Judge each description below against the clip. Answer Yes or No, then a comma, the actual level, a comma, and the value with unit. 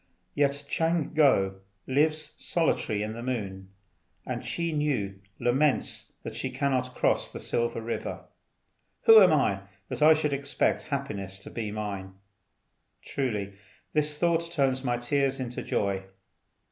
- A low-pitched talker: Yes, low, 130 Hz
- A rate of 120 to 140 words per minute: Yes, slow, 135 wpm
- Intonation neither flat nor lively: No, wide, 5.9 semitones